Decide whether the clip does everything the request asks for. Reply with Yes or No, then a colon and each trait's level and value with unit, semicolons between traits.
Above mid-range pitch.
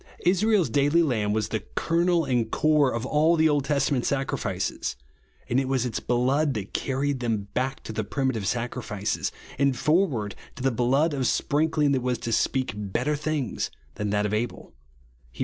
No: low, 130 Hz